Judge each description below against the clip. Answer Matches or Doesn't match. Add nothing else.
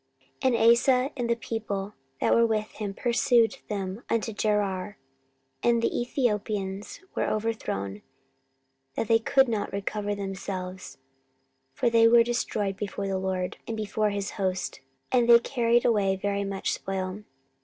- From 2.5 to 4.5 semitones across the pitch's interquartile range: Matches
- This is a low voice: Doesn't match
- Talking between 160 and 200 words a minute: Doesn't match